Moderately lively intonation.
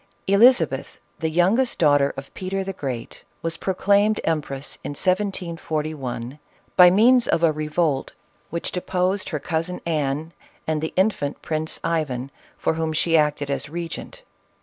Yes: average, 3.8 semitones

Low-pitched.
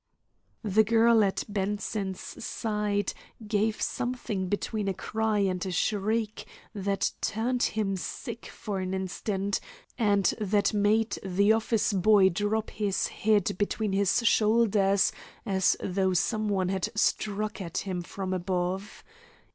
No: high, 205 Hz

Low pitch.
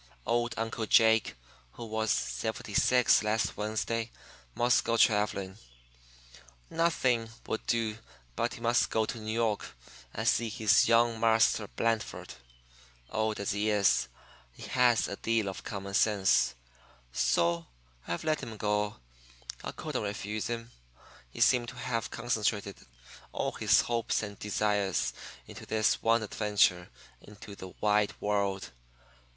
Yes: low, 110 Hz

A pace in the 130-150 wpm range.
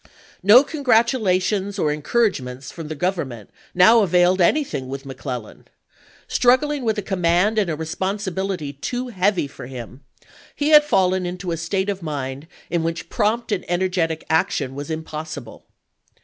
Yes: average, 145 wpm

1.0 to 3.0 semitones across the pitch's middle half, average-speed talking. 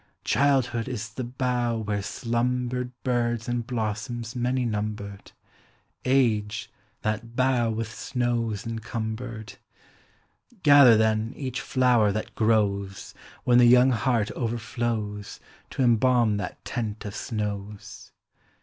No: narrow, 2.4 semitones; slow, 115 wpm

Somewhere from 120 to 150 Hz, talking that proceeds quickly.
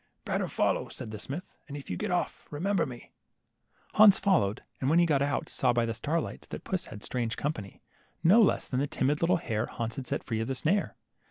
Yes: medium, 140 Hz; fast, 225 wpm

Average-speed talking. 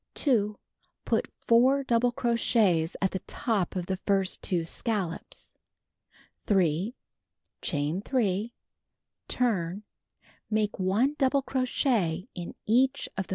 No: slow, 110 wpm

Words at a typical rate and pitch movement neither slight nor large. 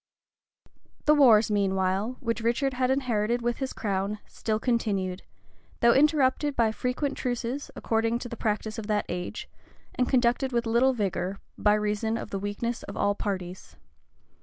Yes: average, 160 wpm; average, 3.4 semitones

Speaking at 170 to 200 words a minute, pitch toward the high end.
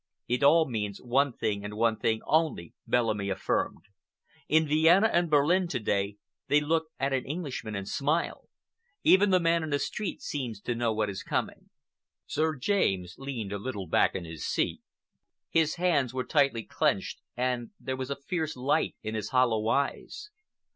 No: average, 175 wpm; low, 130 Hz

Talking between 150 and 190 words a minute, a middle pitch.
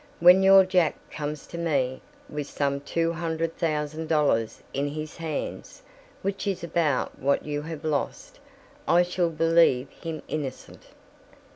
No: average, 140 wpm; medium, 160 Hz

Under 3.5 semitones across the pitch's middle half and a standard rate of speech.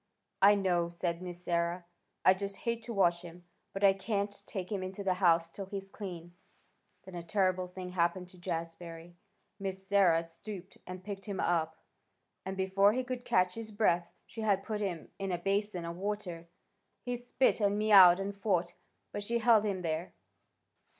Yes: narrow, 2.6 semitones; average, 180 wpm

